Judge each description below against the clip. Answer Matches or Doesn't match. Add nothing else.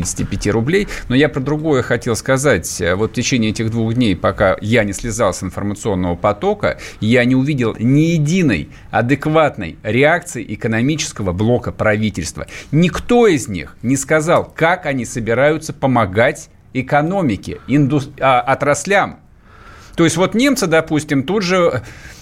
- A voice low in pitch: Matches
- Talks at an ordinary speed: Matches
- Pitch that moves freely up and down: Matches